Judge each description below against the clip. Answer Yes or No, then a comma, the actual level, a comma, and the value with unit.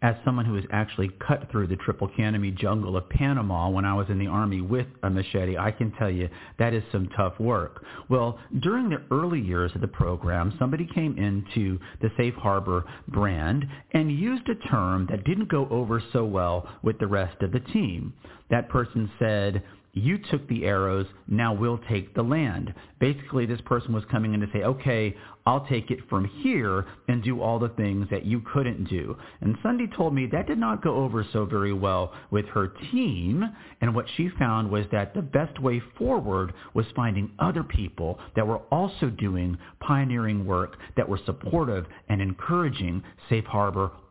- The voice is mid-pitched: No, low, 110 Hz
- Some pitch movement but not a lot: Yes, average, 4.7 semitones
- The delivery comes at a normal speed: Yes, average, 190 wpm